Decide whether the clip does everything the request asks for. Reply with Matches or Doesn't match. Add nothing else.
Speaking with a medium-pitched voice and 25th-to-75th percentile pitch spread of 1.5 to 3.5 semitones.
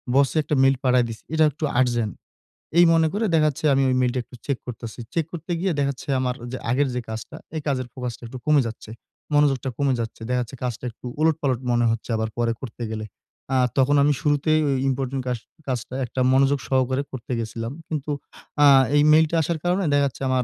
Doesn't match